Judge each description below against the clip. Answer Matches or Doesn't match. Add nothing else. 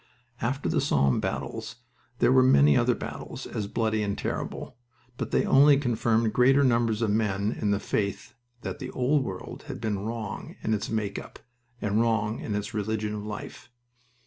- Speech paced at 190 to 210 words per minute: Doesn't match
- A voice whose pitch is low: Matches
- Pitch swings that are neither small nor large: Matches